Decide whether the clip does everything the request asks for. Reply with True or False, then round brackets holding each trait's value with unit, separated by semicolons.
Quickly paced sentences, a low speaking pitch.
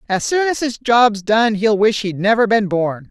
False (230 wpm; 215 Hz)